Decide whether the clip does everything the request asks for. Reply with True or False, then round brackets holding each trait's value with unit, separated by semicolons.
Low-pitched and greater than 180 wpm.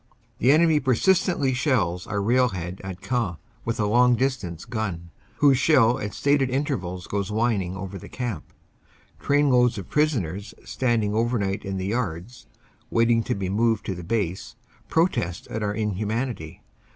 False (110 Hz; 155 wpm)